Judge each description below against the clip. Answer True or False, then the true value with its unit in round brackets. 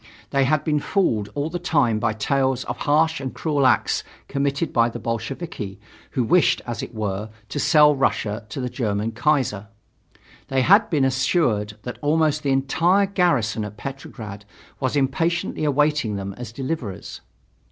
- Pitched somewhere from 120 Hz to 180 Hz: True (135 Hz)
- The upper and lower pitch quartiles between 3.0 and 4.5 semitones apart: False (5.3 semitones)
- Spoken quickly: False (160 wpm)